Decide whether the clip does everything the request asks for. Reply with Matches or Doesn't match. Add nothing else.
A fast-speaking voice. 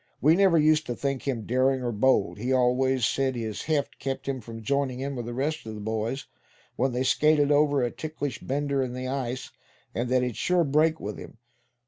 Matches